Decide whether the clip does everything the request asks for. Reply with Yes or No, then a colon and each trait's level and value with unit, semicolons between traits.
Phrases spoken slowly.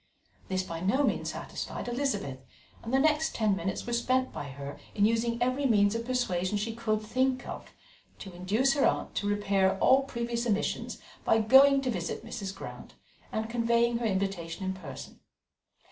No: average, 175 wpm